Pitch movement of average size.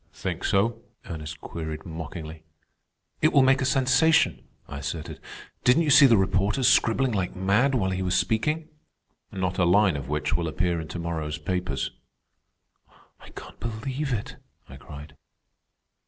No: wide, 8.1 semitones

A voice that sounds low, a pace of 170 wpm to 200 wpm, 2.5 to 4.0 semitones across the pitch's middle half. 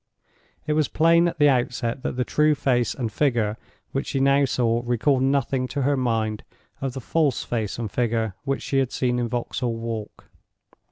Yes: low, 125 Hz; average, 185 wpm; average, 3.0 semitones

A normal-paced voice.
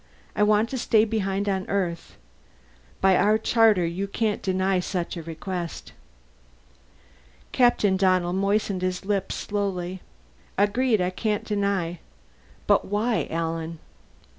No: slow, 120 wpm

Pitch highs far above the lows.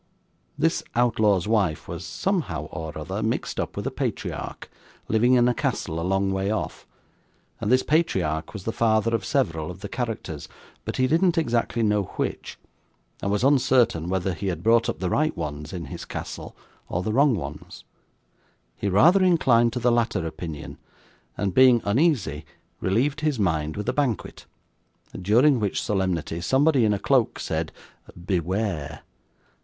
Yes: wide, 5.8 semitones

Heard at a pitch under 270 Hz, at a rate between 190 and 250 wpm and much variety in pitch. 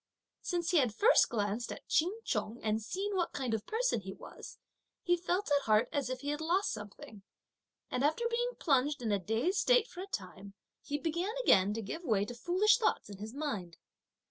No: very high, 285 Hz; fast, 205 wpm; wide, 8.8 semitones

